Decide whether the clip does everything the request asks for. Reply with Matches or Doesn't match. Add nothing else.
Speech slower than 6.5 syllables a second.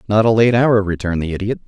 Doesn't match